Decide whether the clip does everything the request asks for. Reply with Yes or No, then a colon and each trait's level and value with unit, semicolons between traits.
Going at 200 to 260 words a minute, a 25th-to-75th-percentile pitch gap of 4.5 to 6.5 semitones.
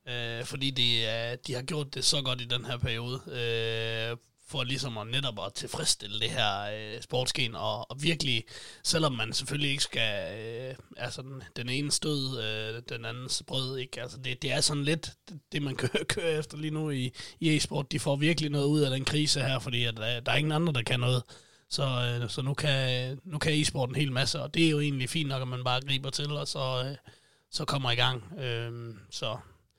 No: average, 220 wpm; average, 3.4 semitones